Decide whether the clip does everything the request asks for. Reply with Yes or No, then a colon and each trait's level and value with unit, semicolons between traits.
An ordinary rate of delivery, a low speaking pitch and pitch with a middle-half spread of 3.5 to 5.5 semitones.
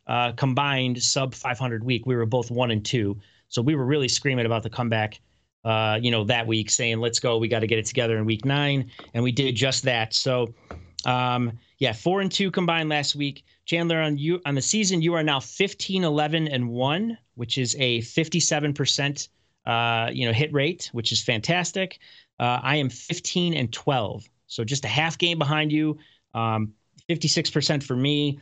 Yes: average, 195 wpm; low, 130 Hz; average, 4.5 semitones